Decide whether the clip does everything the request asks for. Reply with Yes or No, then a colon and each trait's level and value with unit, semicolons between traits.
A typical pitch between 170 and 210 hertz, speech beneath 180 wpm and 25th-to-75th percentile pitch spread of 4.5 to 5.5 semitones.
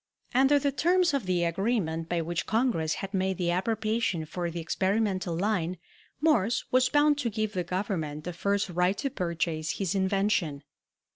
Yes: high, 190 Hz; average, 165 wpm; average, 4.8 semitones